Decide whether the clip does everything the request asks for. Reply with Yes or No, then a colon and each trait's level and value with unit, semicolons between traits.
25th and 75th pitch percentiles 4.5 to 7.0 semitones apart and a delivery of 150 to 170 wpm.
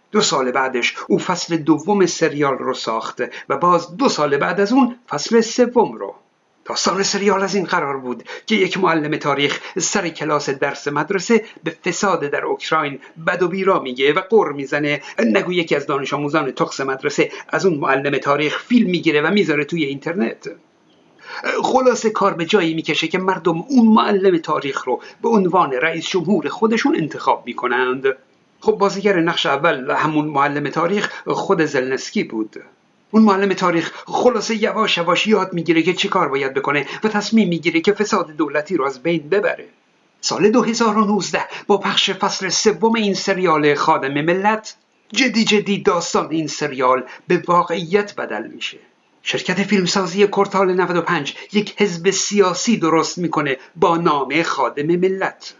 Yes: average, 5.1 semitones; fast, 155 wpm